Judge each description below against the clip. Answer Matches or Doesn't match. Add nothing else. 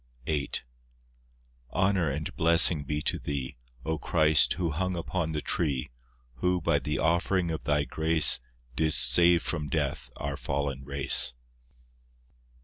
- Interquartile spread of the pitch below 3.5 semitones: Matches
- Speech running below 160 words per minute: Matches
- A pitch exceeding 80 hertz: Doesn't match